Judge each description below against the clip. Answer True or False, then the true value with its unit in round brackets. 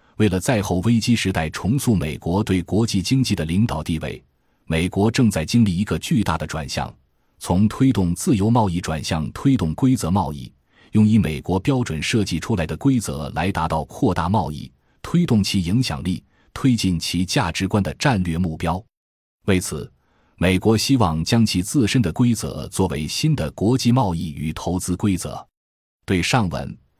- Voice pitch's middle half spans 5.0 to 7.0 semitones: True (5.3 semitones)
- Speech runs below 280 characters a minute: True (260 characters per minute)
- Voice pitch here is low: True (95 Hz)